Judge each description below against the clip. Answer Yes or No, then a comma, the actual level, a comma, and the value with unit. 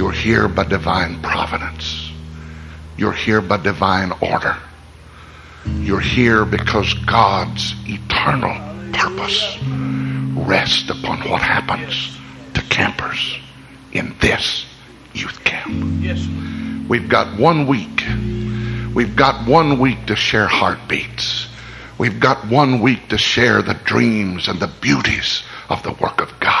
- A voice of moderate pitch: No, low, 100 Hz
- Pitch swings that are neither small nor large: No, wide, 6.2 semitones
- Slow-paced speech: Yes, slow, 120 wpm